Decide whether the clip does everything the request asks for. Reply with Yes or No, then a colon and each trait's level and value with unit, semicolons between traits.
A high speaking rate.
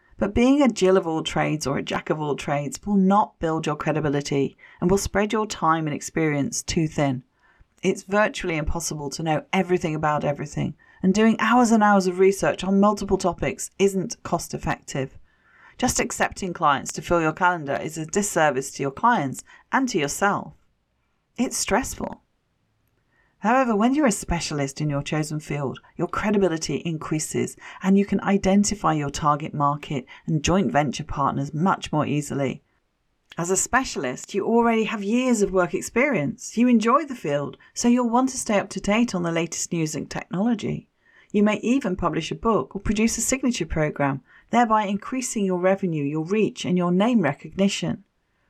No: average, 175 wpm